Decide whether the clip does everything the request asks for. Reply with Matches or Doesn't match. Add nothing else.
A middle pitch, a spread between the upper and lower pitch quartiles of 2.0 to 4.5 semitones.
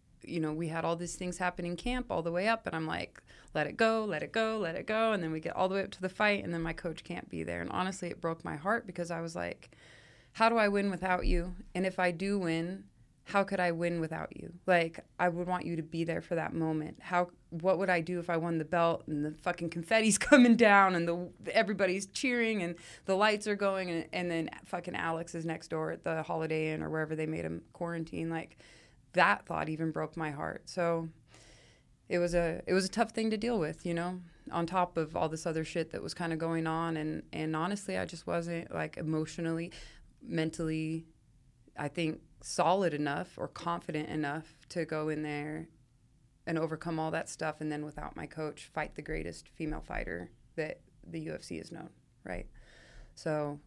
Matches